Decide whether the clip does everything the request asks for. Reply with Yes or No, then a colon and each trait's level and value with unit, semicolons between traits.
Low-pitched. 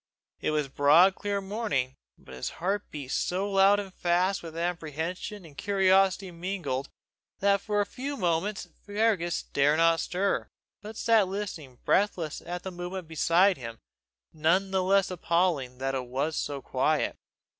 No: medium, 180 Hz